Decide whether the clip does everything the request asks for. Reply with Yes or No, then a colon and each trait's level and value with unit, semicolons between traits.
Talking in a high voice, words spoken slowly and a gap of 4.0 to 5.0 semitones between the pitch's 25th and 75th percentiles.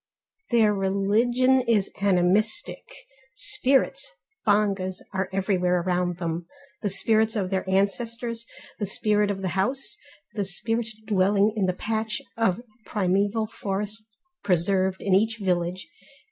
No: high, 200 Hz; slow, 120 wpm; average, 2.9 semitones